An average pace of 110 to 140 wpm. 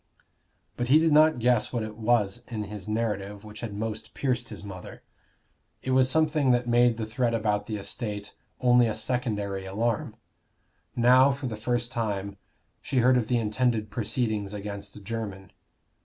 No: average, 165 wpm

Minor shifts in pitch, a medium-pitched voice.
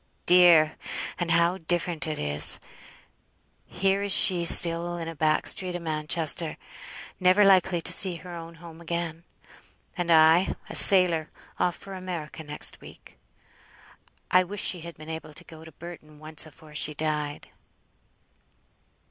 Yes: narrow, 2.2 semitones; medium, 170 Hz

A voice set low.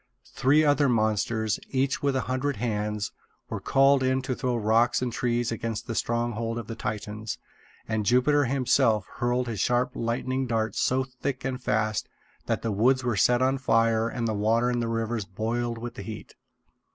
Yes: low, 120 Hz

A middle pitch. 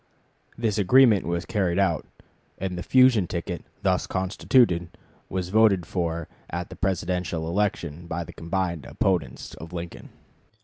No: very low, 90 Hz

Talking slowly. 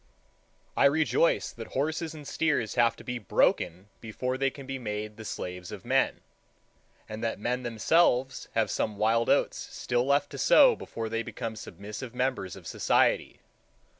No: average, 165 wpm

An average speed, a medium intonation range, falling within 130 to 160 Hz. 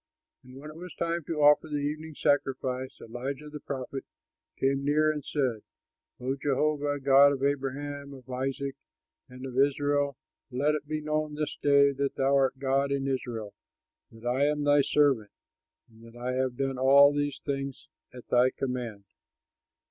No: average, 165 wpm; narrow, 1.9 semitones; medium, 140 Hz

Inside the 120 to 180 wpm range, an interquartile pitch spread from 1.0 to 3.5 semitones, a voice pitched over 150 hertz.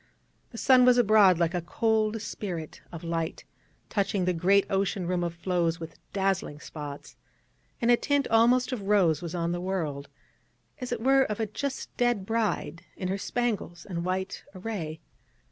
No: average, 170 wpm; average, 4.7 semitones; high, 190 Hz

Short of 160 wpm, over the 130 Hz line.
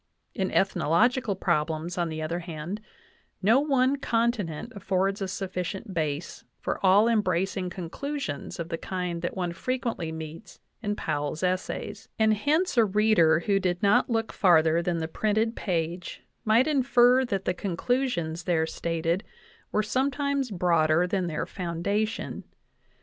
Yes: average, 145 wpm; high, 190 Hz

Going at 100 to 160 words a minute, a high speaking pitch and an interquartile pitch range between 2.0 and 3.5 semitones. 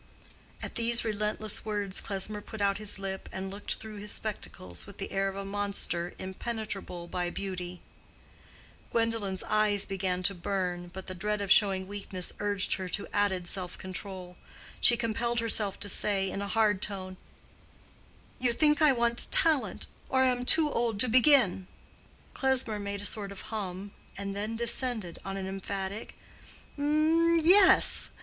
Yes: average, 155 wpm; high, 205 Hz; average, 3.2 semitones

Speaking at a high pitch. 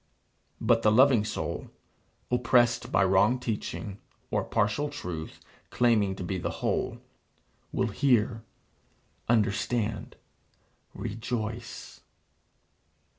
No: low, 110 Hz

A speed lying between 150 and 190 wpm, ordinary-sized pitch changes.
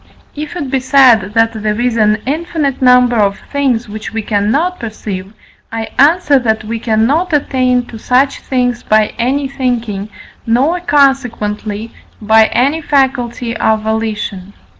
No: average, 140 wpm; average, 3.9 semitones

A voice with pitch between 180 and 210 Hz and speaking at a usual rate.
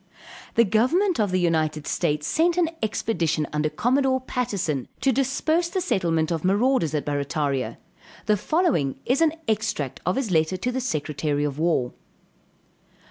Yes: high, 190 Hz; average, 150 wpm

